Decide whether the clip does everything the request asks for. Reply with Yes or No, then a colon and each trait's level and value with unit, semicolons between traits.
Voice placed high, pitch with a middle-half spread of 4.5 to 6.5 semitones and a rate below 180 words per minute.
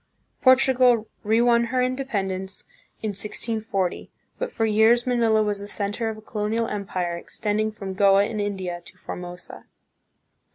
No: high, 215 Hz; average, 2.9 semitones; average, 150 wpm